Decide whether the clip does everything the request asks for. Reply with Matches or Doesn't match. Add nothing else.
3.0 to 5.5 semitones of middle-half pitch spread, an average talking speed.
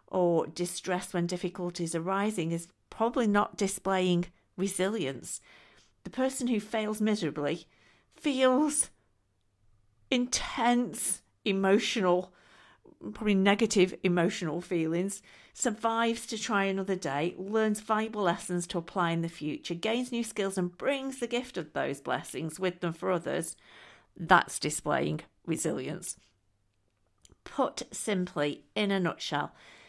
Doesn't match